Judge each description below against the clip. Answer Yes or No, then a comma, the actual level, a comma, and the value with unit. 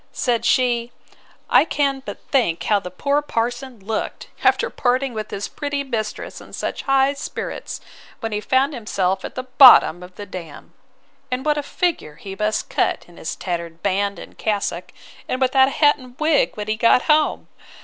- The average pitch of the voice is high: Yes, high, 240 Hz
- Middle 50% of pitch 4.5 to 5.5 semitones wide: Yes, average, 5.2 semitones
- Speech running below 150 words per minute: No, average, 180 wpm